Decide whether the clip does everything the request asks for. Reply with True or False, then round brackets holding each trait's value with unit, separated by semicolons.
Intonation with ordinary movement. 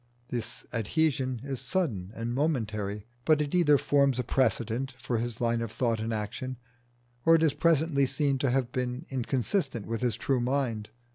True (3.4 semitones)